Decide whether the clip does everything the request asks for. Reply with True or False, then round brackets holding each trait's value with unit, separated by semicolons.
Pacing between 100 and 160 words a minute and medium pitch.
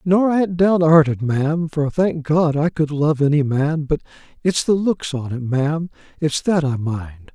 False (195 wpm; 155 Hz)